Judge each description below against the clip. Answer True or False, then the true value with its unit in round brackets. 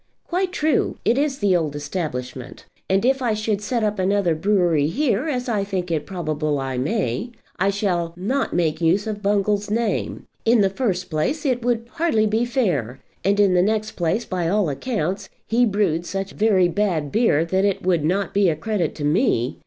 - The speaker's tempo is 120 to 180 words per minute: False (190 wpm)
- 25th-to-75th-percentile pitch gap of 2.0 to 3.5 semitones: False (4.9 semitones)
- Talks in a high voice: True (195 Hz)